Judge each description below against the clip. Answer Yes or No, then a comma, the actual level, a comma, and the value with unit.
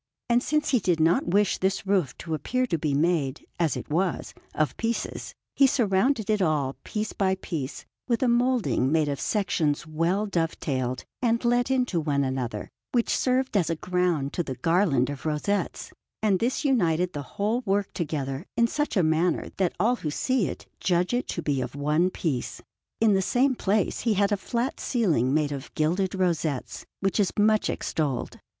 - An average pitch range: No, wide, 6.2 semitones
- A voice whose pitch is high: No, medium, 180 Hz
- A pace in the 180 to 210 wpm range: Yes, average, 185 wpm